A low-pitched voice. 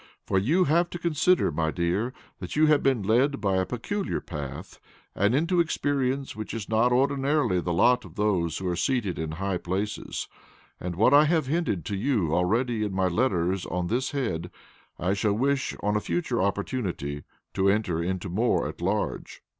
Yes: low, 105 Hz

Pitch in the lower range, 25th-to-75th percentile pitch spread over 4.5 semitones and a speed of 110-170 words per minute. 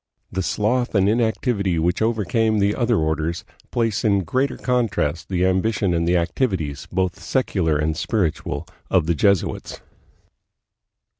Yes: very low, 95 Hz; average, 4.9 semitones; slow, 135 wpm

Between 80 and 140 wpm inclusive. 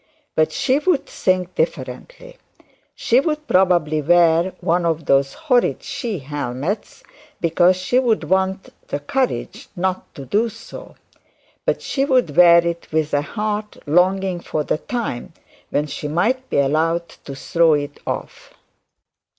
Yes: slow, 135 wpm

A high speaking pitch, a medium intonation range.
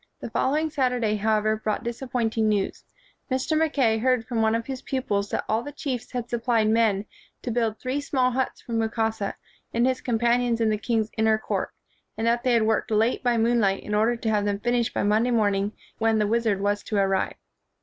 No: high, 225 Hz; narrow, 2.3 semitones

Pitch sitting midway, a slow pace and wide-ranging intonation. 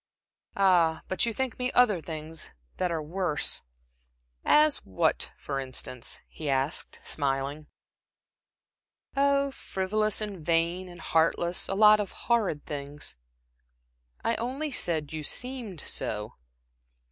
Yes: medium, 175 Hz; slow, 120 wpm; wide, 6.2 semitones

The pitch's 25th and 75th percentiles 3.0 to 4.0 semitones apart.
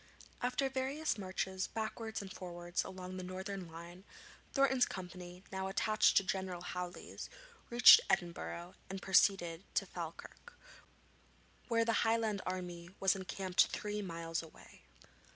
Yes: average, 3.5 semitones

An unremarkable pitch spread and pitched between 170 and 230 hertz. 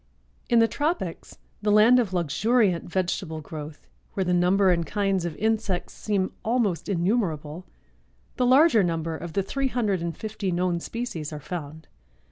Yes: average, 4.7 semitones; medium, 185 Hz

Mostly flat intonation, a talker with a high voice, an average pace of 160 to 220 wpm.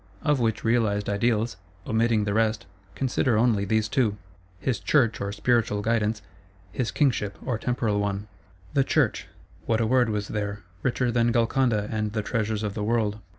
No: narrow, 2.3 semitones; low, 110 Hz; average, 165 wpm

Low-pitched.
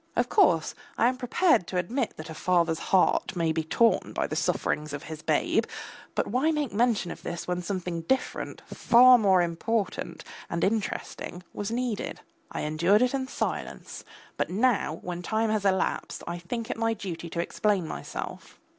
No: high, 195 Hz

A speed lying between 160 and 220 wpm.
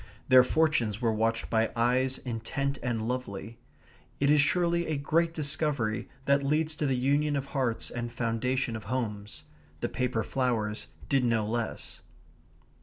No: average, 150 wpm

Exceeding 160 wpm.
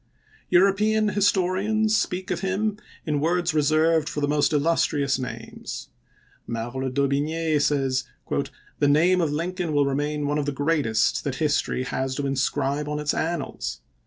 No: average, 155 wpm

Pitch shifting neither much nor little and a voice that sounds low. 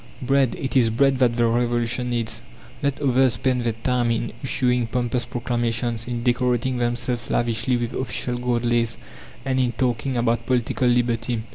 No: narrow, 1.3 semitones; low, 120 Hz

